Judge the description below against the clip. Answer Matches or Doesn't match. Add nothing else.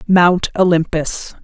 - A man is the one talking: Doesn't match